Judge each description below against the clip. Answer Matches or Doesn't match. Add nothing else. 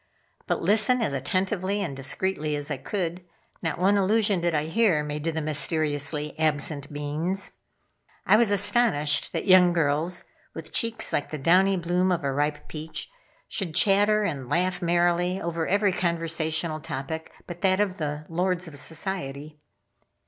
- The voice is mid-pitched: Matches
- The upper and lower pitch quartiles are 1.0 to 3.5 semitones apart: Doesn't match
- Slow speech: Doesn't match